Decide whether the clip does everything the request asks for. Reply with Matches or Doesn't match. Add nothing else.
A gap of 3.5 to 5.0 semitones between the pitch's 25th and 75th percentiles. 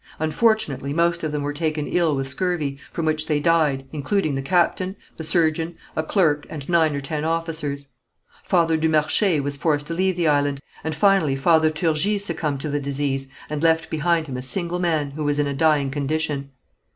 Doesn't match